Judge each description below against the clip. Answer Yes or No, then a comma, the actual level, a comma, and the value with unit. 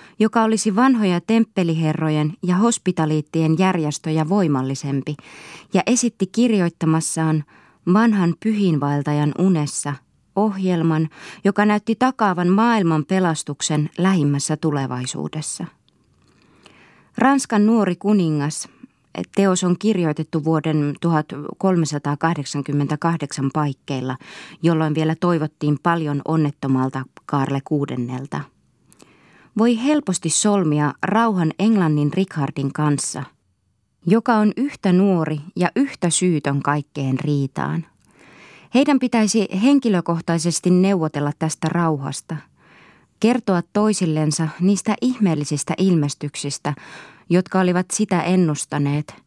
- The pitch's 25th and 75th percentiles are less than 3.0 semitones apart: No, average, 4.8 semitones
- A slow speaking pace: Yes, slow, 85 wpm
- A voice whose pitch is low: No, medium, 165 Hz